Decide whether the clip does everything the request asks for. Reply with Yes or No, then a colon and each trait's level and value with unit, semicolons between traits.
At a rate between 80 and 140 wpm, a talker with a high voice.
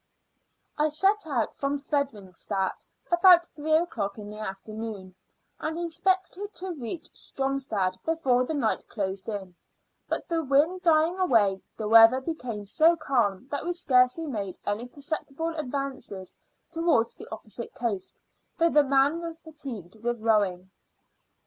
Yes: slow, 135 wpm; very high, 270 Hz